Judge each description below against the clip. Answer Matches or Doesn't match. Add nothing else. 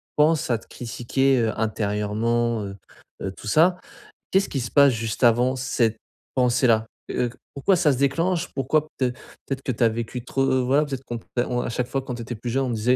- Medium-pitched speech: Doesn't match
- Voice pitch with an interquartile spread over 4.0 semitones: Doesn't match